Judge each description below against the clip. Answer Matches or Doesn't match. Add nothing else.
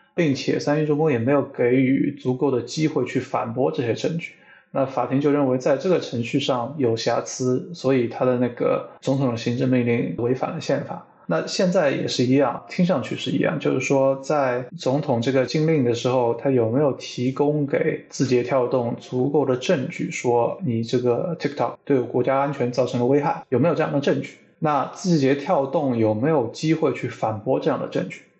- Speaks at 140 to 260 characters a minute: Doesn't match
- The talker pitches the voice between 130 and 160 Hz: Matches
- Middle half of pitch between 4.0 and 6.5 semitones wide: Doesn't match